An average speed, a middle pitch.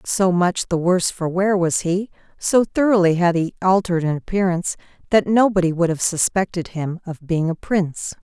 Yes: average, 180 wpm; medium, 180 Hz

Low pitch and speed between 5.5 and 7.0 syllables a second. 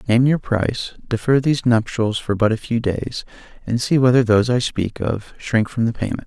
No: low, 115 Hz; 5.3 syllables/s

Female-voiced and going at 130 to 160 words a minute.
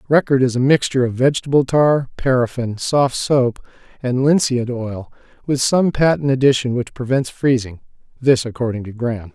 No: male; average, 150 wpm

